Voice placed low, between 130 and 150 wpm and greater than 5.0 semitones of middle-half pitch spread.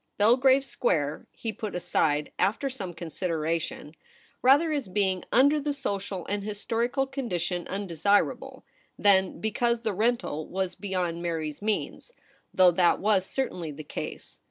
No: high, 200 Hz; slow, 135 wpm; wide, 5.4 semitones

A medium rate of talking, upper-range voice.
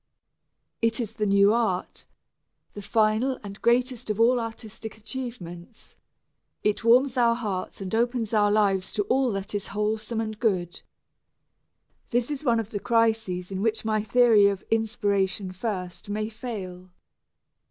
Yes: average, 145 wpm; high, 215 Hz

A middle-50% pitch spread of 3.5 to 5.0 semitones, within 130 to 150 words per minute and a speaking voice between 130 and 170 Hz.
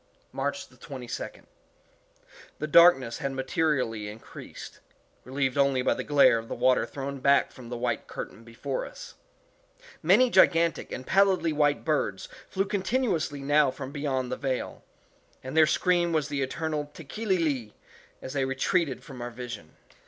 Yes: average, 4.5 semitones; average, 145 wpm; medium, 140 Hz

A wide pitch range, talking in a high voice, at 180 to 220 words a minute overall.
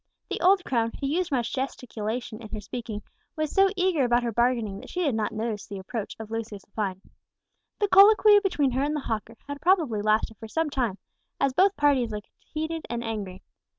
Yes: wide, 6.1 semitones; high, 240 Hz; average, 195 wpm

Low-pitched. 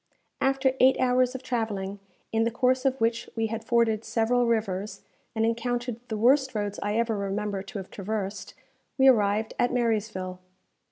No: high, 225 Hz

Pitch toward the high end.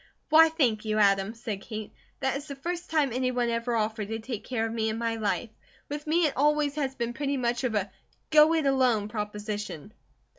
Yes: high, 240 Hz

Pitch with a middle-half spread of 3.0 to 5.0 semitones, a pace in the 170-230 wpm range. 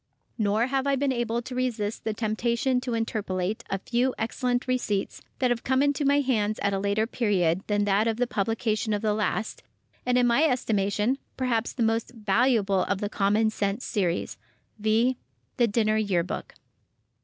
Yes: average, 3.3 semitones; average, 180 wpm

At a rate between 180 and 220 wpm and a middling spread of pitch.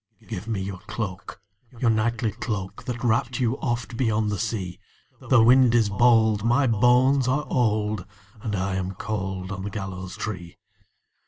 No: average, 160 wpm; average, 3.6 semitones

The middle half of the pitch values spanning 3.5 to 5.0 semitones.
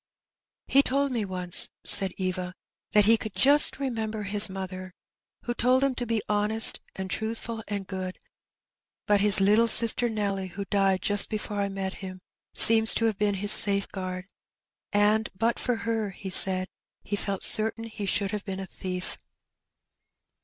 No: narrow, 2.6 semitones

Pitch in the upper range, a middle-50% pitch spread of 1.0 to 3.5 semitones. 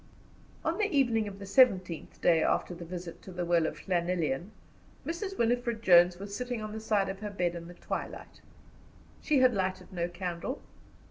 No: high, 195 Hz; average, 4.7 semitones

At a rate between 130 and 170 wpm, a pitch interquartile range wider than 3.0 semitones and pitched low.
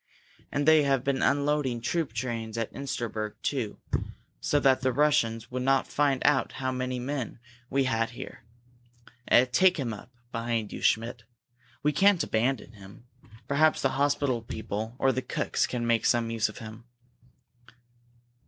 Yes: average, 155 wpm; average, 3.5 semitones; low, 130 Hz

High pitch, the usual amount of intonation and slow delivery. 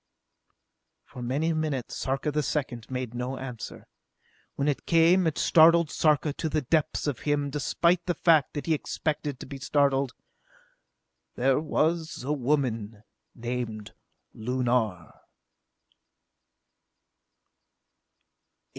No: medium, 140 Hz; average, 3.8 semitones; slow, 115 wpm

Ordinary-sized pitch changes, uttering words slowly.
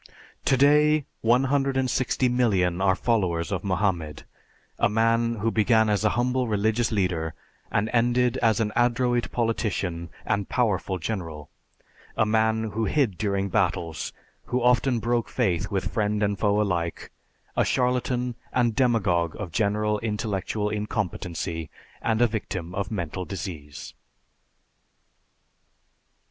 Yes: average, 4.3 semitones; slow, 120 wpm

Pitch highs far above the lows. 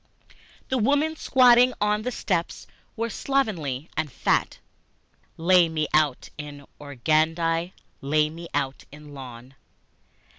Yes: wide, 6.9 semitones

